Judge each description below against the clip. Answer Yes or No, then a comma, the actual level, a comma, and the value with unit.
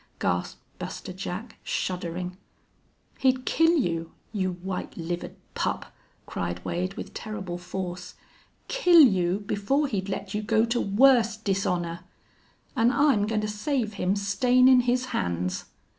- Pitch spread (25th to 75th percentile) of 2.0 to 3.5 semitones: No, average, 5.2 semitones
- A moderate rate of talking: No, slow, 130 wpm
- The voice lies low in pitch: No, high, 200 Hz